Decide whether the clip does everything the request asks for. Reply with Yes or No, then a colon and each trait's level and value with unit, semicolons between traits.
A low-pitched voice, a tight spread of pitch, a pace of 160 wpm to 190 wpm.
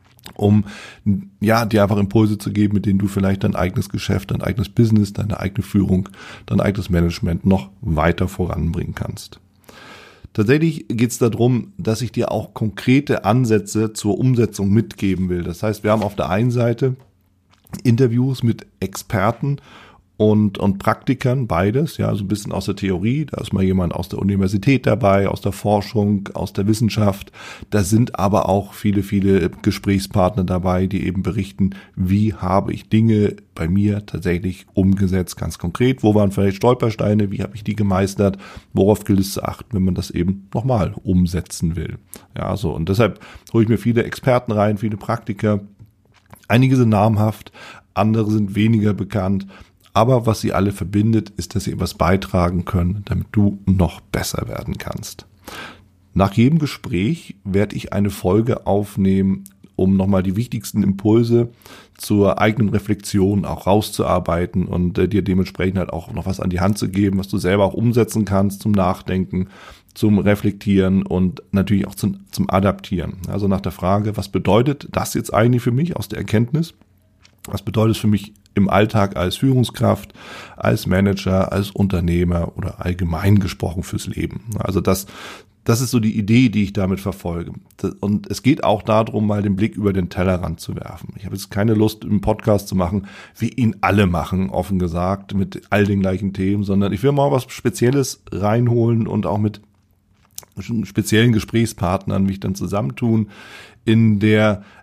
Yes: low, 100 Hz; narrow, 2.3 semitones; average, 170 wpm